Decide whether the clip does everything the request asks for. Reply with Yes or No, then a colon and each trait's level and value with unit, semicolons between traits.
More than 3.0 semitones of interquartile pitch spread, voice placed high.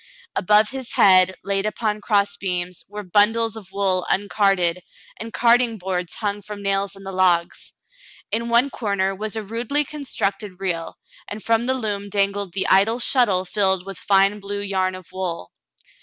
No: narrow, 2.4 semitones; high, 200 Hz